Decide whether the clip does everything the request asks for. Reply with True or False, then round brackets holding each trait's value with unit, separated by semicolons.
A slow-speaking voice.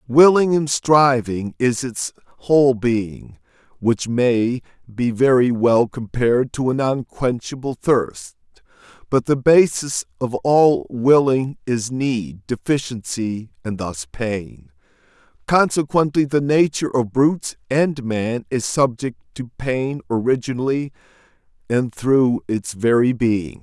True (115 wpm)